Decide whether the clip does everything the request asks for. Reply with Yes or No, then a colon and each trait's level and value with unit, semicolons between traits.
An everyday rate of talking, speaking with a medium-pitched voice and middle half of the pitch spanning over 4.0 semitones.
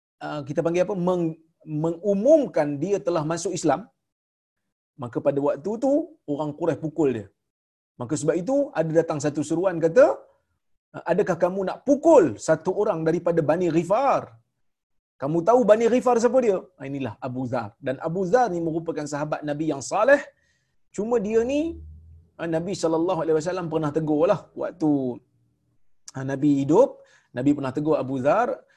No: fast, 145 wpm; medium, 160 Hz; average, 5.0 semitones